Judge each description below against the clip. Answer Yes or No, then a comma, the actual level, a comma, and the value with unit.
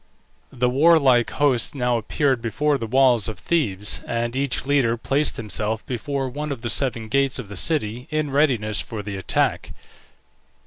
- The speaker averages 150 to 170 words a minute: Yes, average, 165 wpm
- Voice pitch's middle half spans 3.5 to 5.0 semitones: Yes, average, 3.8 semitones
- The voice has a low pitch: Yes, low, 125 Hz